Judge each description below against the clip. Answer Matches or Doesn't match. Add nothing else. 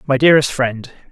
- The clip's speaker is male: Matches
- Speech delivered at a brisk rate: Doesn't match